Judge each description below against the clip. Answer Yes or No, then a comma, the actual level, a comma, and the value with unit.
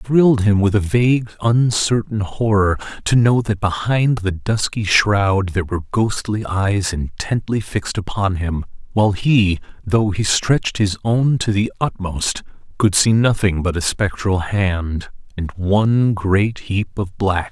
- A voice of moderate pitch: No, low, 105 Hz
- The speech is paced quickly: No, average, 160 wpm